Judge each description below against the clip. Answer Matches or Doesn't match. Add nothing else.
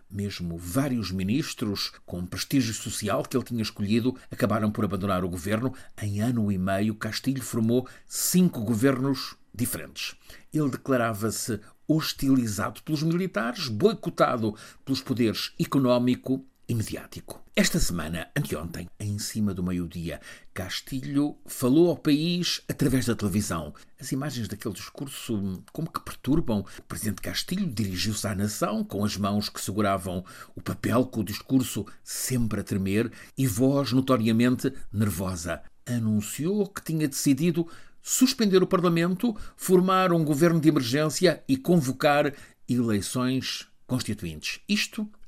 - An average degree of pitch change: Doesn't match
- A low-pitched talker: Matches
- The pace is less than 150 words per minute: Matches